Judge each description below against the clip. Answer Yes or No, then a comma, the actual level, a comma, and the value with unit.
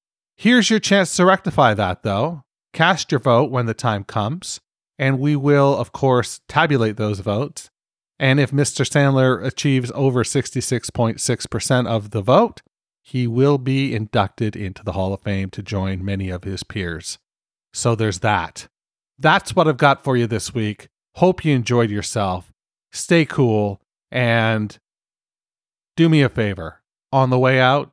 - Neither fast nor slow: Yes, average, 155 wpm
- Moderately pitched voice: No, low, 125 Hz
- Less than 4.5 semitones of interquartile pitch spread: No, average, 5.1 semitones